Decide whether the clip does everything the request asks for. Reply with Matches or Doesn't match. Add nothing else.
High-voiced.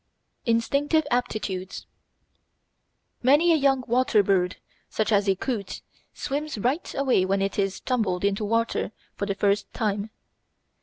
Matches